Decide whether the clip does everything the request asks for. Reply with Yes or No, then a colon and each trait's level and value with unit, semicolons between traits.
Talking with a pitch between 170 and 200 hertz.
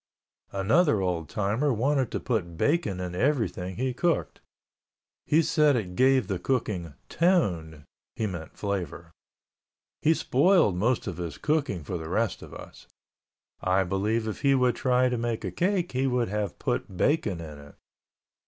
No: low, 110 Hz